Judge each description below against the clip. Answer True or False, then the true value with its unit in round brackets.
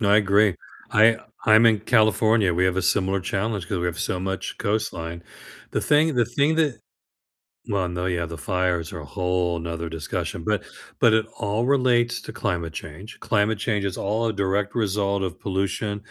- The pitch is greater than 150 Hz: False (100 Hz)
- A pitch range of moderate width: True (3.4 semitones)